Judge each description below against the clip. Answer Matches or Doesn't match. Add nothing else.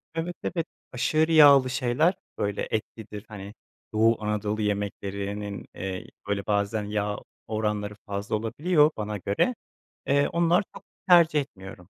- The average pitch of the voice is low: Matches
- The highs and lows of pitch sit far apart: Matches